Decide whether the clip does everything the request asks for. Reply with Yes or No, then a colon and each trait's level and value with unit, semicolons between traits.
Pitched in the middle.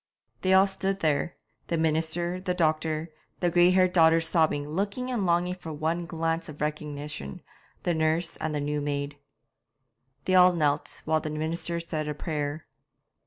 Yes: medium, 160 Hz